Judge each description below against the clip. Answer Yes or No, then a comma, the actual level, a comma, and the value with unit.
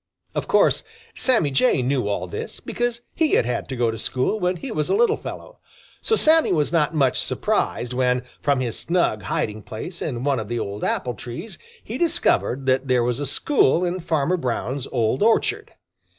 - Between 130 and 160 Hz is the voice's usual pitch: Yes, medium, 140 Hz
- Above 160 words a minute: Yes, average, 195 wpm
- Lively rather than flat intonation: Yes, wide, 7.0 semitones